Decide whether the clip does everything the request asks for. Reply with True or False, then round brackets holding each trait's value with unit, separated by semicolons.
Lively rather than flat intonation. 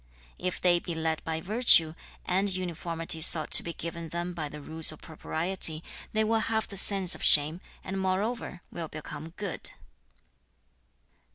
False (3.0 semitones)